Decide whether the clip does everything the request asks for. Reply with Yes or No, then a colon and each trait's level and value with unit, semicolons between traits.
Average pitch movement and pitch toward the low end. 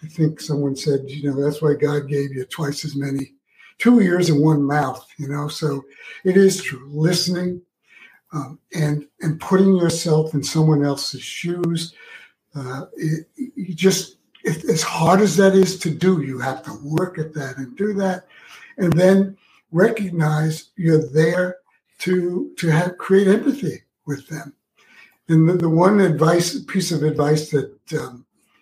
No: average, 3.9 semitones; medium, 160 Hz